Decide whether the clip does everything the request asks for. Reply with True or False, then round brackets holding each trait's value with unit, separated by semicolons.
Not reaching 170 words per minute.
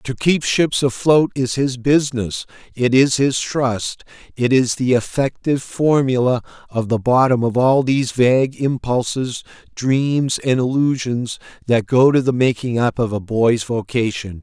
True (155 wpm)